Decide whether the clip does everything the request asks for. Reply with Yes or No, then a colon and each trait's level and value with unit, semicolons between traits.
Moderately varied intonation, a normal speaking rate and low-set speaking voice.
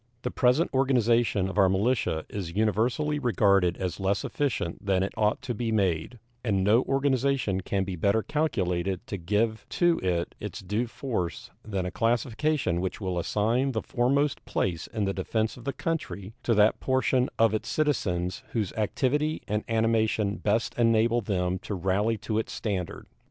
Yes: average, 4.4 semitones; average, 165 wpm; low, 110 Hz